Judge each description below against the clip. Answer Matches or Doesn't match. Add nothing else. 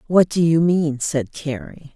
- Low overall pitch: Doesn't match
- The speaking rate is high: Doesn't match